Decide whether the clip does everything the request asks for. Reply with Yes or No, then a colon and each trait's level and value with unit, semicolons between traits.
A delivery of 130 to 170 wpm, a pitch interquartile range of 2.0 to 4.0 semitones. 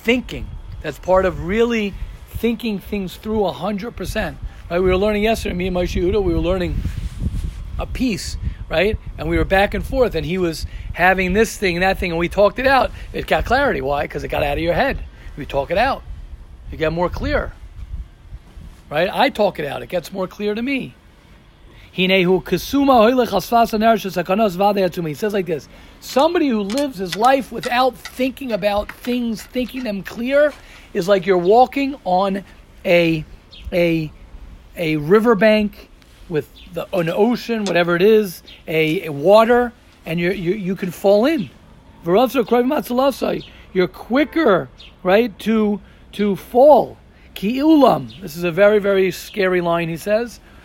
No: average, 155 wpm; average, 4.4 semitones